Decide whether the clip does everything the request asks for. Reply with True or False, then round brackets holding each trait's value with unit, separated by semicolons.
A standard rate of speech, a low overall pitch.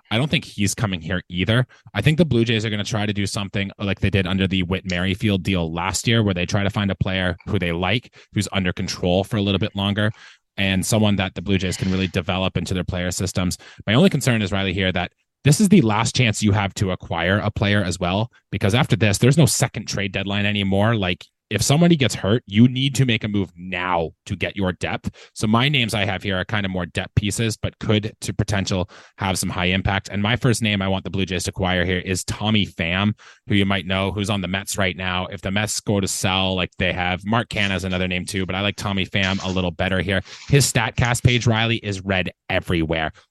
False (250 wpm; 100 Hz)